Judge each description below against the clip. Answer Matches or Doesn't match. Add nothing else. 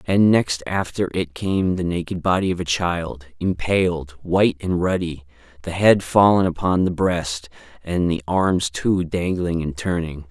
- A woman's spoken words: Doesn't match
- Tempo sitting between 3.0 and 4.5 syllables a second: Matches